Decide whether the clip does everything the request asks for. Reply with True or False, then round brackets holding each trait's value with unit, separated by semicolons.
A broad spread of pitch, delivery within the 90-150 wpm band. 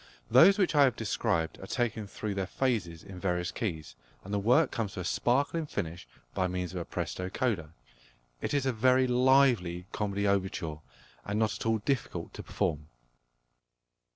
False (6.0 semitones; 175 wpm)